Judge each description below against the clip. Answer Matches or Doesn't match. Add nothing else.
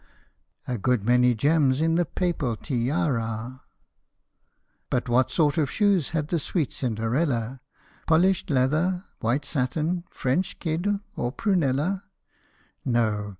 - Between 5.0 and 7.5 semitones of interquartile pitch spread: Matches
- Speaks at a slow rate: Matches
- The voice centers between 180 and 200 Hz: Doesn't match